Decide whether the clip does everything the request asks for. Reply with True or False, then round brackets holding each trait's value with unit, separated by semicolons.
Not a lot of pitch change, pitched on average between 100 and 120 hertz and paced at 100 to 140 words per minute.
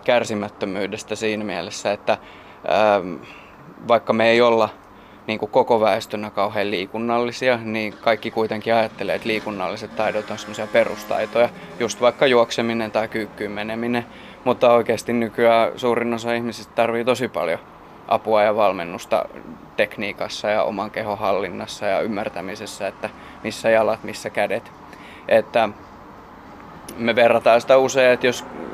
True (1.9 semitones; 110 Hz; 130 wpm)